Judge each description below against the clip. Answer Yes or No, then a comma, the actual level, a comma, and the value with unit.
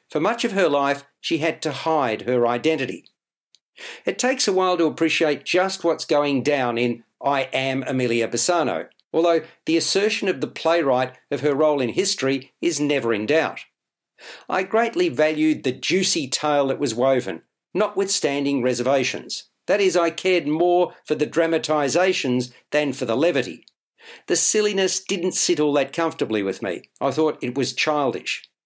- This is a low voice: No, medium, 155 Hz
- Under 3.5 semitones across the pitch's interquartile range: No, average, 4.8 semitones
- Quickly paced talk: No, average, 165 wpm